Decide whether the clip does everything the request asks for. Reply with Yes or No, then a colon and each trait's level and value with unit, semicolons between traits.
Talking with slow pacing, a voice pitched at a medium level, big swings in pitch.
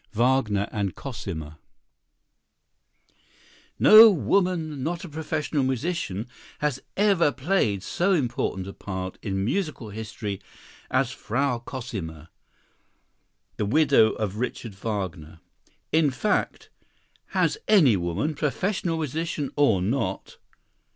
No: slow, 105 wpm; low, 130 Hz; wide, 7.8 semitones